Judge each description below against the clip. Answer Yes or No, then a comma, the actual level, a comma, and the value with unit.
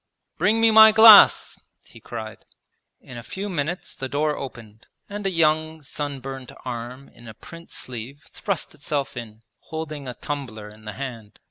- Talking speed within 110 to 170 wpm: Yes, average, 160 wpm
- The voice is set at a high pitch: No, medium, 140 Hz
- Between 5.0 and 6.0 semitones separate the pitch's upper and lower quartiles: Yes, average, 5.3 semitones